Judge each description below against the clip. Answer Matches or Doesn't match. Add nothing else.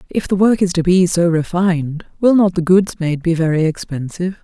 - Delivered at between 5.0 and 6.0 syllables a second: Matches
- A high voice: Doesn't match